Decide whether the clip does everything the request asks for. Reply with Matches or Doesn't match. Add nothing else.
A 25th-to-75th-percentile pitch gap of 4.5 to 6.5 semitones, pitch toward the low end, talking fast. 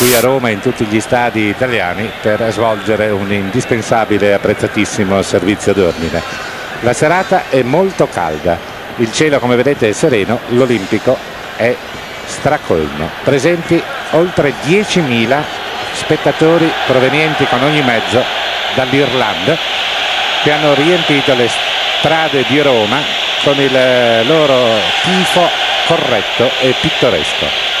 Doesn't match